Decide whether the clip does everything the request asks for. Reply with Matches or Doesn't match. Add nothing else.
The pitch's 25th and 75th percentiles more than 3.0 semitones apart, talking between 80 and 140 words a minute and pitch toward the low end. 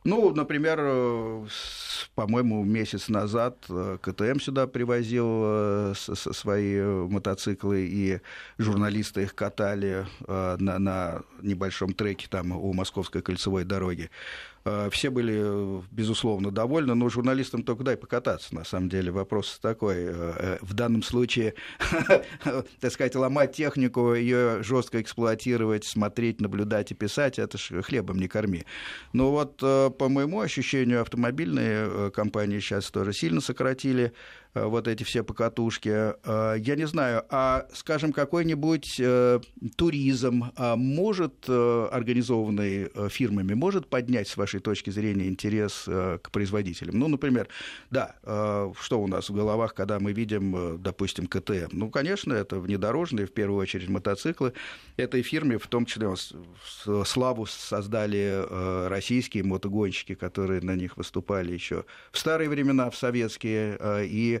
Matches